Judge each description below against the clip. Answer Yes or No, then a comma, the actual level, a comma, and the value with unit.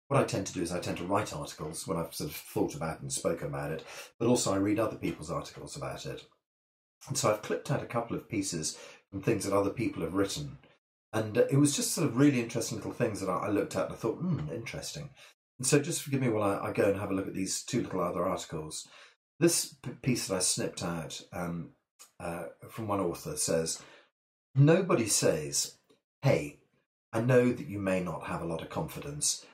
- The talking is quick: Yes, fast, 225 wpm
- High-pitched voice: No, low, 115 Hz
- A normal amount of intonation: No, wide, 7.3 semitones